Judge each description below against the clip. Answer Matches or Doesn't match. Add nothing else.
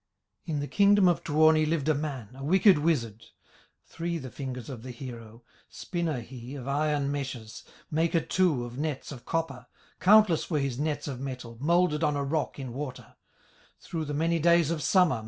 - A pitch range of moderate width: Matches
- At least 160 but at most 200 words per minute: Matches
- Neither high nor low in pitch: Matches